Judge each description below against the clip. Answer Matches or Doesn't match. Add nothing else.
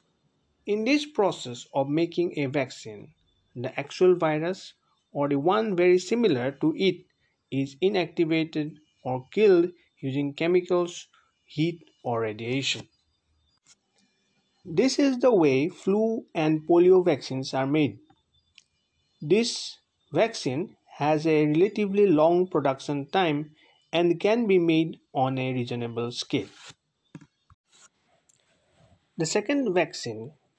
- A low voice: Doesn't match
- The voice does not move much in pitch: Doesn't match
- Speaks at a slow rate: Matches